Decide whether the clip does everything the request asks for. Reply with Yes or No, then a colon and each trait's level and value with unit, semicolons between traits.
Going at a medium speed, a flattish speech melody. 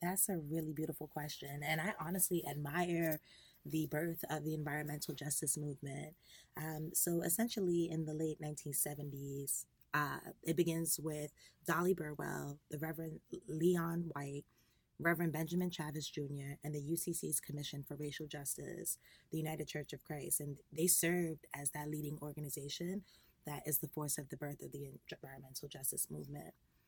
Yes: average, 150 wpm; narrow, 2.1 semitones